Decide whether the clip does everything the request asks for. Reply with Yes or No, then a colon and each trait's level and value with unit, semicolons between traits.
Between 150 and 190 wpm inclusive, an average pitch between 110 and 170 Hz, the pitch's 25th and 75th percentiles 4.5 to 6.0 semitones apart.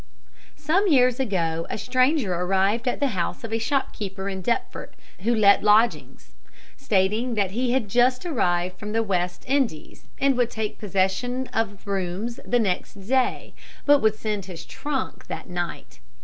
No: average, 160 wpm; high, 215 Hz; average, 4.8 semitones